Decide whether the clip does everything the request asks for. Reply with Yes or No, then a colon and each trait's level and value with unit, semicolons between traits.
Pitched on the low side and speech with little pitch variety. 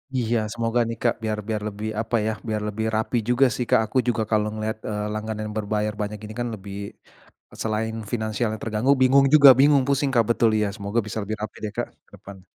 Yes: low, 110 Hz; narrow, 2.0 semitones